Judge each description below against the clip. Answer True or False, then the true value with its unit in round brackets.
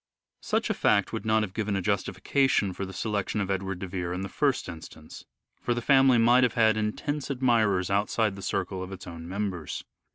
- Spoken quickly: True (225 wpm)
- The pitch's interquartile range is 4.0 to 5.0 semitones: False (3.4 semitones)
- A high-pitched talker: False (100 Hz)